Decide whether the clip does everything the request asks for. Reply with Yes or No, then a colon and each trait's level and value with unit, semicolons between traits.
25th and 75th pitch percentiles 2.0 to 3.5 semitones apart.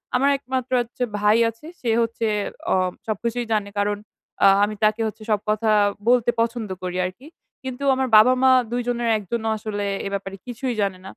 Yes: average, 2.9 semitones